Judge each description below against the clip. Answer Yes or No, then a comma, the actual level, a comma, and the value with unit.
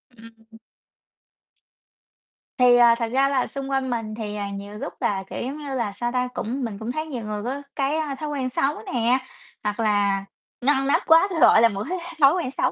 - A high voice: Yes, high, 245 Hz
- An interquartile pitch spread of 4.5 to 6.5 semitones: No, average, 4.0 semitones